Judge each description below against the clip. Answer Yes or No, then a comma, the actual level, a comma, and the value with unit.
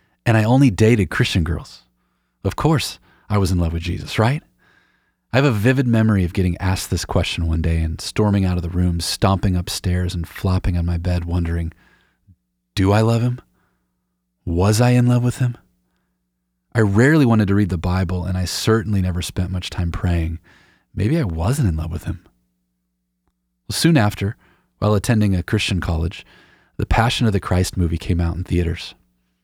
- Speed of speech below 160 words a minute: No, average, 185 wpm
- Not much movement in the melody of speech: No, average, 4.2 semitones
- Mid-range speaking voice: No, very low, 90 Hz